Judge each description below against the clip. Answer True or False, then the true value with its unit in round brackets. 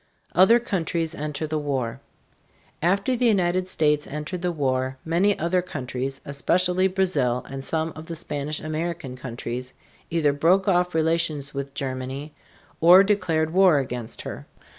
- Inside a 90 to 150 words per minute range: True (140 wpm)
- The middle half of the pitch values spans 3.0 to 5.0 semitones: True (4.4 semitones)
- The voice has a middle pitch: True (155 Hz)